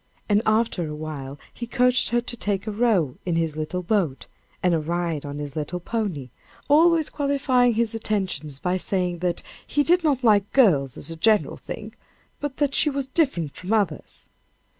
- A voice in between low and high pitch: No, high, 200 Hz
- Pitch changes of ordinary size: No, wide, 7.1 semitones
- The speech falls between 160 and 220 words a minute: Yes, average, 180 wpm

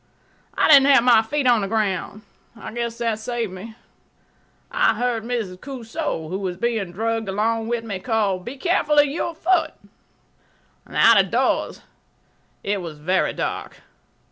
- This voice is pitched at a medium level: No, high, 225 Hz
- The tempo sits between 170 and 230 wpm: No, average, 155 wpm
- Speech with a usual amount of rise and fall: Yes, average, 3.9 semitones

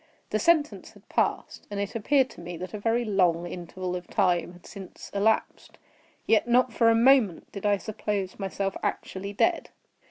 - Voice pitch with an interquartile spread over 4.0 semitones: No, average, 3.7 semitones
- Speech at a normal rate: Yes, average, 180 wpm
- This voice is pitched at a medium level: No, high, 200 Hz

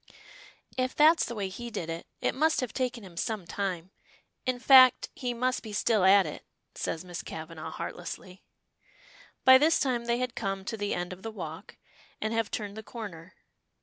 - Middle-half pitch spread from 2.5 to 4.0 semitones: No, average, 5.2 semitones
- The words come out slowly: No, average, 185 wpm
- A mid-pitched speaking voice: No, high, 215 Hz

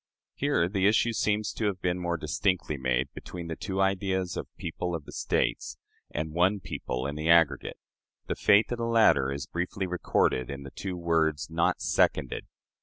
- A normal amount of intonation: Yes, average, 4.0 semitones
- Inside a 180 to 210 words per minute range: Yes, average, 185 wpm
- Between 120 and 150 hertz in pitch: No, very low, 85 Hz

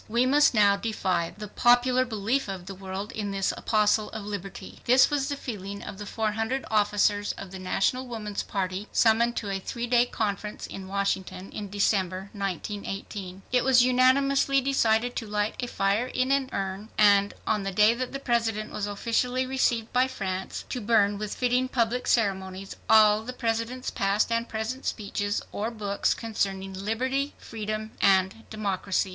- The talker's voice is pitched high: Yes, high, 215 Hz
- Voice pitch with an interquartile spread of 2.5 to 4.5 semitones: Yes, average, 3.5 semitones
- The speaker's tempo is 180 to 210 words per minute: No, average, 170 wpm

